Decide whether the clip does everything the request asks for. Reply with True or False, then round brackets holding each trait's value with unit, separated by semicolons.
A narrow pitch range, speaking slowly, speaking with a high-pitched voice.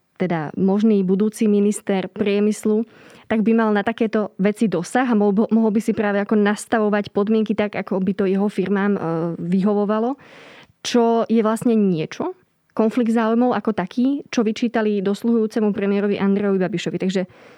False (2.2 semitones; 145 wpm; 210 Hz)